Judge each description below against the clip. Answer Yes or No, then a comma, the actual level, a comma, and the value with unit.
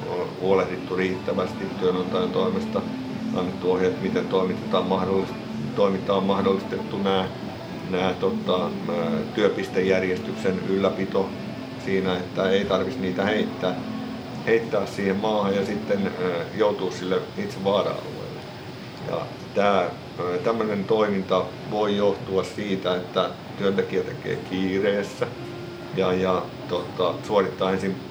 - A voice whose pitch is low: Yes, very low, 95 Hz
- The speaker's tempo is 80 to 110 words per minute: Yes, average, 100 wpm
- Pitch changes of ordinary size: No, narrow, 1.8 semitones